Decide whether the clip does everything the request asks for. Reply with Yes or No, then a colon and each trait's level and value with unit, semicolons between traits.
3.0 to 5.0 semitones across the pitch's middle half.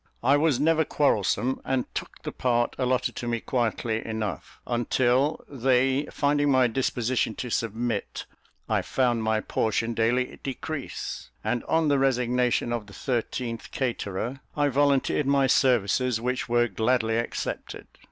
No: narrow, 2.5 semitones